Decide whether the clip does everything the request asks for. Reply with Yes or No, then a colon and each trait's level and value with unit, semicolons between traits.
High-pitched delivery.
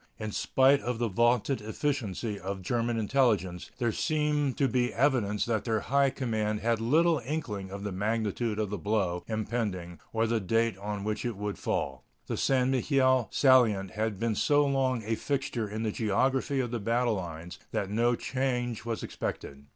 No: low, 115 Hz